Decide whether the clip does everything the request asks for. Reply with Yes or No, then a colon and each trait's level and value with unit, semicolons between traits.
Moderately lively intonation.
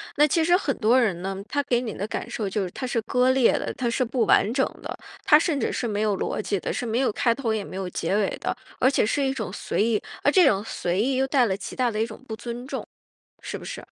Yes: average, 4.0 semitones